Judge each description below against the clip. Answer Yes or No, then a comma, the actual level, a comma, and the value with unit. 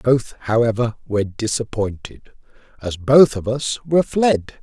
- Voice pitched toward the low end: Yes, low, 120 Hz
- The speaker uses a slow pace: Yes, slow, 130 wpm